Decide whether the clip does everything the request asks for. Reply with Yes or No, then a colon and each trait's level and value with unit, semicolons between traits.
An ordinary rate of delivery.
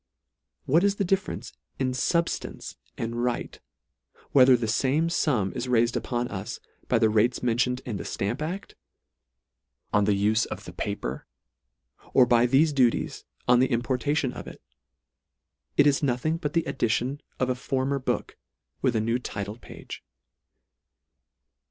Yes: average, 150 wpm